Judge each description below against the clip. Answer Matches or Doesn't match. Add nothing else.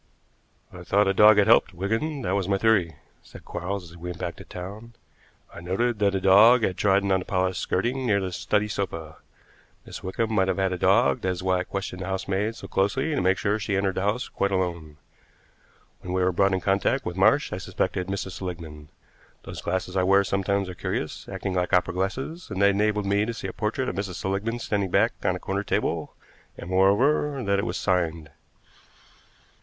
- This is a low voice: Matches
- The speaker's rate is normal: Doesn't match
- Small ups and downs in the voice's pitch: Matches